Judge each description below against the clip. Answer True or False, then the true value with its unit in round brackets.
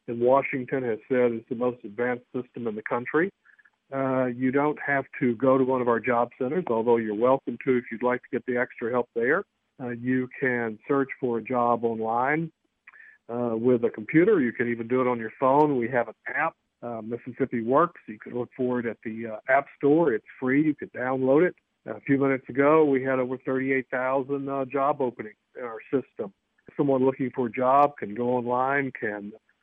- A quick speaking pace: True (215 wpm)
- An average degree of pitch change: False (2.1 semitones)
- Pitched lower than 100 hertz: False (125 Hz)